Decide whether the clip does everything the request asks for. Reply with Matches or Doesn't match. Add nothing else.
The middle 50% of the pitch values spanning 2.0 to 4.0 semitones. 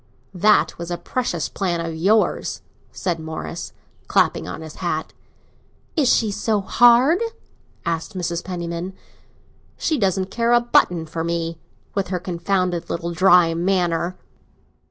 Matches